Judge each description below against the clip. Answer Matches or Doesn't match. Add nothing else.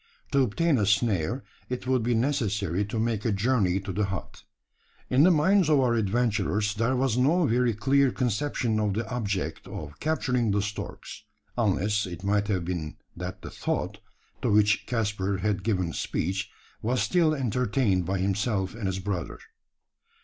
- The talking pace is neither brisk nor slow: Matches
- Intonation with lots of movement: Doesn't match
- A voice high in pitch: Doesn't match